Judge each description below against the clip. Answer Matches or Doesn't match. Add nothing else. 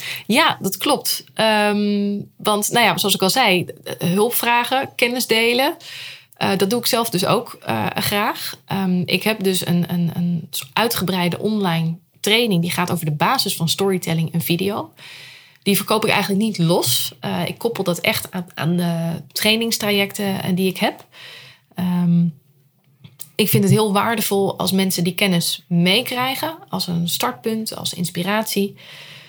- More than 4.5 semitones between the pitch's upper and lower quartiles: Doesn't match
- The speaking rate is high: Doesn't match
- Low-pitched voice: Doesn't match